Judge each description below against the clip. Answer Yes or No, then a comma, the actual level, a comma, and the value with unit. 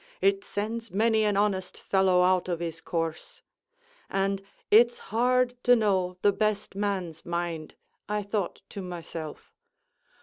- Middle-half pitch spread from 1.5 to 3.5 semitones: Yes, average, 3.2 semitones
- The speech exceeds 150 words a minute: No, slow, 135 wpm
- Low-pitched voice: No, high, 195 Hz